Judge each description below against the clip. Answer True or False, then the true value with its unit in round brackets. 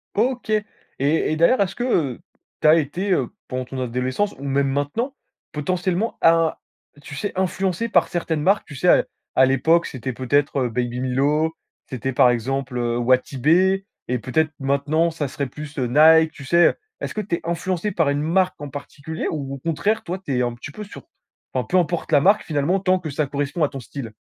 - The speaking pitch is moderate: True (150 Hz)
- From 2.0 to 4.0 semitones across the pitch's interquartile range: False (4.7 semitones)